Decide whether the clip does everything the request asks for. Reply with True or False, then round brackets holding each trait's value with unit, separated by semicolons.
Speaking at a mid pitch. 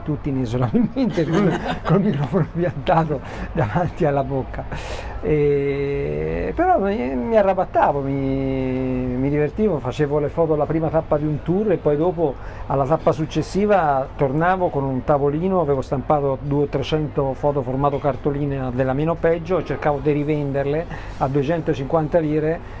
True (150 Hz)